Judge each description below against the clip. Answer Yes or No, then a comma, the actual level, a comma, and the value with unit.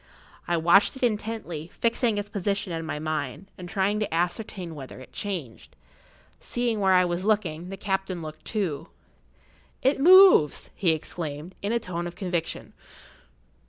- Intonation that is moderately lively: Yes, average, 4.2 semitones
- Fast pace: No, average, 155 wpm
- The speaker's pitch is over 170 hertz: Yes, medium, 185 Hz